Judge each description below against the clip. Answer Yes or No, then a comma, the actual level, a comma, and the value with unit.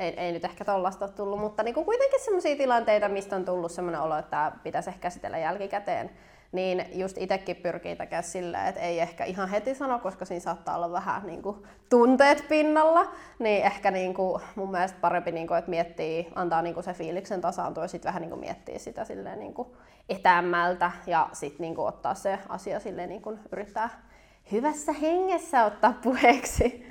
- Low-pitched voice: No, high, 195 Hz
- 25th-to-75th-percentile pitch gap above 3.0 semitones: Yes, average, 5.2 semitones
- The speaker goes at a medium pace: No, fast, 175 wpm